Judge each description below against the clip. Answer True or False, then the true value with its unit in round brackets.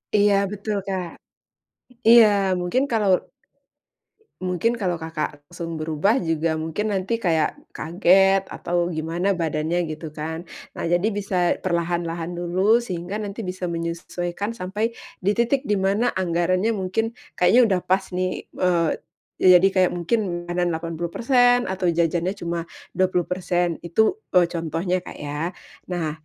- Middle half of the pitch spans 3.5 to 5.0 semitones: False (2.8 semitones)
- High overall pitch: False (180 Hz)